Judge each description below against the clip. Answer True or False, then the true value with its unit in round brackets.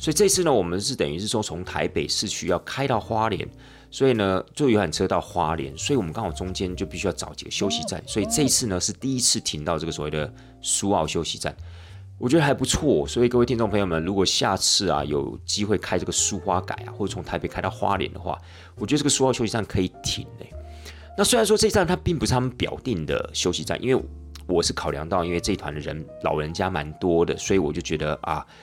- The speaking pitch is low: True (95 Hz)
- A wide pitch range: True (6.1 semitones)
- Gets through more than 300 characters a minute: True (355 characters per minute)